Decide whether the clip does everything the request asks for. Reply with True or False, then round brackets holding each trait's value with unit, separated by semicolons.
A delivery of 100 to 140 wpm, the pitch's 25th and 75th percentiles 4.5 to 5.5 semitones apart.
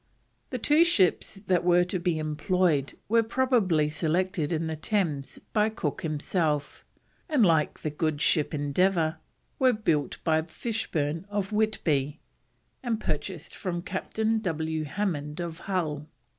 True (135 wpm; 5.0 semitones)